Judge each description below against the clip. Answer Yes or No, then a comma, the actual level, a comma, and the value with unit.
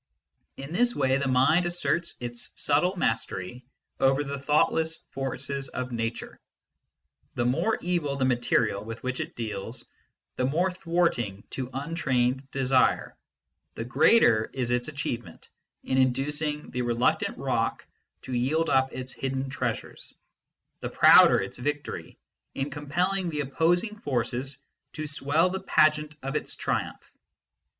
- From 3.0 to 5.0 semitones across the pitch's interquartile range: Yes, average, 3.7 semitones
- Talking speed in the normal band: No, slow, 130 wpm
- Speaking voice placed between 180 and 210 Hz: No, low, 135 Hz